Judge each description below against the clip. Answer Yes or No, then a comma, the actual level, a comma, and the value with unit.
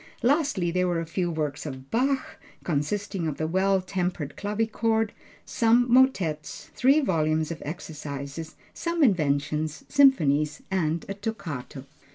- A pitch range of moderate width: No, wide, 6.5 semitones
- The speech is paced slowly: Yes, slow, 130 wpm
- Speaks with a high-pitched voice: No, medium, 175 Hz